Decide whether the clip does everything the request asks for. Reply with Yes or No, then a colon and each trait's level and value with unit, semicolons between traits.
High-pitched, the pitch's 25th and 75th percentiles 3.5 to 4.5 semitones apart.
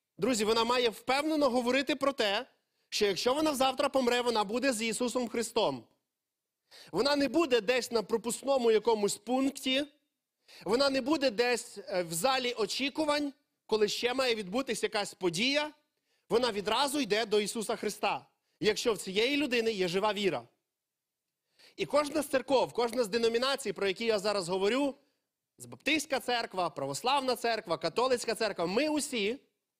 Yes: high, 240 Hz; average, 4.2 semitones